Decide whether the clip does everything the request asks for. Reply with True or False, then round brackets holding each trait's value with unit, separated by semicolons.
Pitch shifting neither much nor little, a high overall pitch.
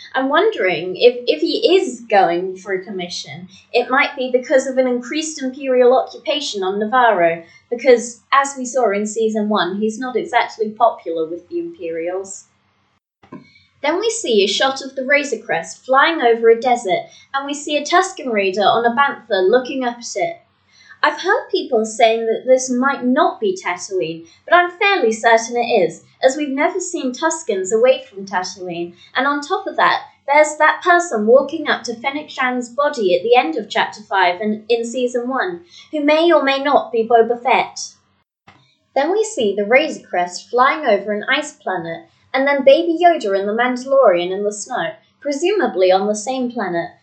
False (6.3 semitones; 255 Hz)